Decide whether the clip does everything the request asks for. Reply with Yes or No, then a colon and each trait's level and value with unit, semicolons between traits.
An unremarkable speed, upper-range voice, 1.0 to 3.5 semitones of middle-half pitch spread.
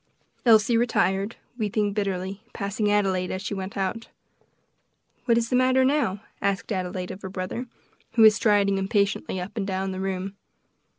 Yes: average, 160 wpm; high, 200 Hz; narrow, 2.4 semitones